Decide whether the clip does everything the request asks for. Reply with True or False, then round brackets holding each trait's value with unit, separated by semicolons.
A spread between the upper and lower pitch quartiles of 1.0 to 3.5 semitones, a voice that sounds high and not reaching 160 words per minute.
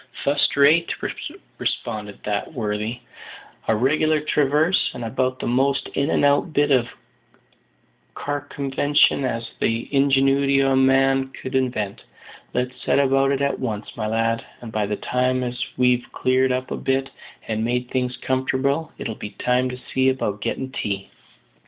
False (2.7 semitones; 130 Hz; 150 wpm)